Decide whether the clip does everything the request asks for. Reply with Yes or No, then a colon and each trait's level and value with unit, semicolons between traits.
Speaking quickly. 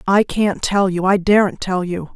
No: average, 195 wpm